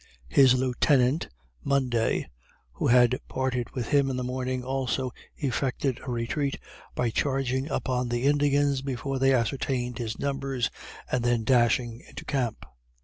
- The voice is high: No, low, 130 Hz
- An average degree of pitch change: No, narrow, 1.9 semitones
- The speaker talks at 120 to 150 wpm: Yes, average, 140 wpm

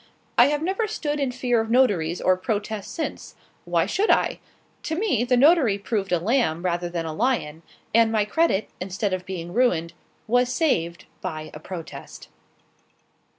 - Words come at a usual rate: Yes, average, 165 wpm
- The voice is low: No, high, 215 Hz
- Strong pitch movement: Yes, wide, 6.6 semitones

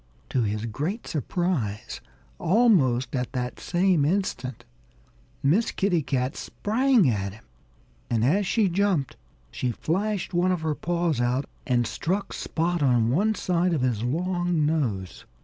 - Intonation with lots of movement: Yes, wide, 6.7 semitones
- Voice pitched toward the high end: No, medium, 160 Hz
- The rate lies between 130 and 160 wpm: Yes, average, 140 wpm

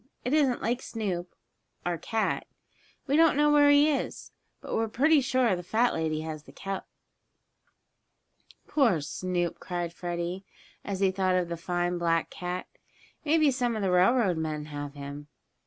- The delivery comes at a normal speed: Yes, average, 160 wpm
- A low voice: No, medium, 185 Hz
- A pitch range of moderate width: No, wide, 6.5 semitones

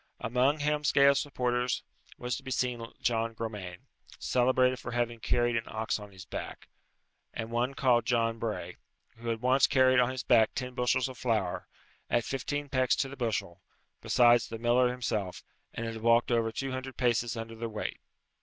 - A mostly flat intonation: Yes, narrow, 2.1 semitones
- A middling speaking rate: Yes, average, 175 wpm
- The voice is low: Yes, low, 120 Hz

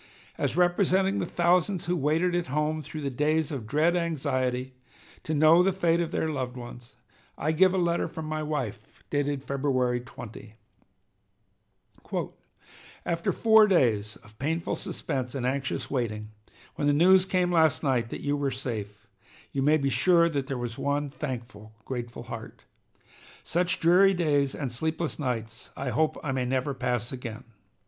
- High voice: No, medium, 145 Hz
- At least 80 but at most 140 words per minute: No, average, 160 wpm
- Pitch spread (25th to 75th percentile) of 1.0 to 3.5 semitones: No, average, 5.0 semitones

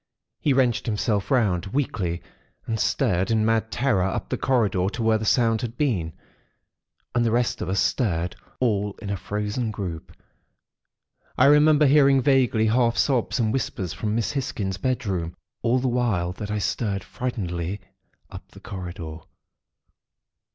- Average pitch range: Yes, average, 4.5 semitones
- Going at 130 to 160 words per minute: Yes, average, 150 wpm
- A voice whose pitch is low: Yes, low, 110 Hz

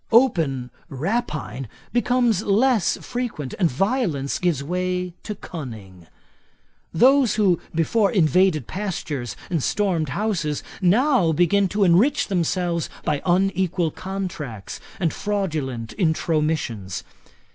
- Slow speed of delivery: Yes, slow, 105 wpm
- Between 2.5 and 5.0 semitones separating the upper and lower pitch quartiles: No, wide, 5.4 semitones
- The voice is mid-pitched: Yes, medium, 175 Hz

